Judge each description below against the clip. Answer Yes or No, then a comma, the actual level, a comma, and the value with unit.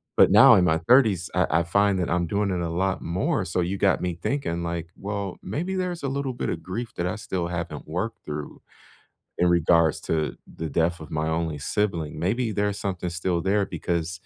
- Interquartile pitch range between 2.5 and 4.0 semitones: Yes, average, 3.4 semitones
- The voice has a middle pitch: No, very low, 90 Hz